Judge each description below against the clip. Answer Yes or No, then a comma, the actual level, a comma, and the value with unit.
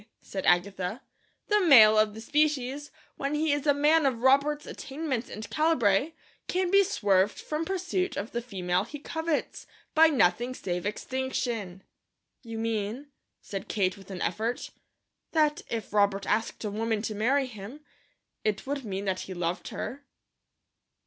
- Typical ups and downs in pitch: No, wide, 6.5 semitones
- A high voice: Yes, high, 235 Hz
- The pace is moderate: Yes, average, 155 wpm